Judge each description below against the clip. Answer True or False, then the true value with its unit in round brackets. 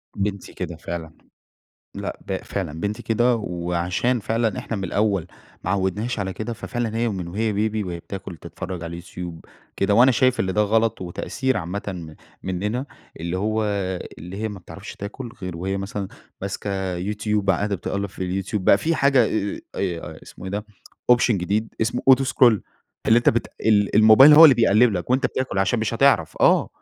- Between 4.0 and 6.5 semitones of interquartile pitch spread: False (3.6 semitones)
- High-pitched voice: False (100 Hz)